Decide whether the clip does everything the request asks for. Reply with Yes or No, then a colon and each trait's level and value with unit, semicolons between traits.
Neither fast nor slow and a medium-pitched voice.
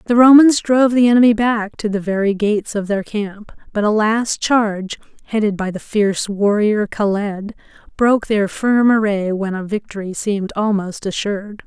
No: average, 170 wpm; high, 210 Hz